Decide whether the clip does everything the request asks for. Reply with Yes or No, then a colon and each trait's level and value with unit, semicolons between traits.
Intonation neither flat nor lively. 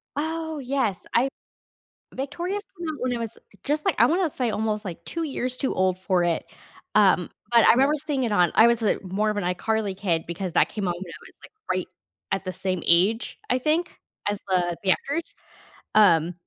No: wide, 6.7 semitones